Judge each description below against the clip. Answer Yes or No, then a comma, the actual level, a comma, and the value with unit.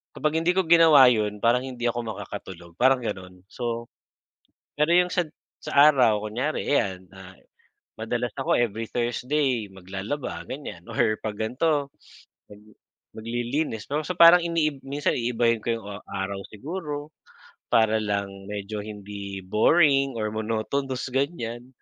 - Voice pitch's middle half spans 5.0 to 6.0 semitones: Yes, wide, 5.4 semitones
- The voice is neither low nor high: No, low, 120 Hz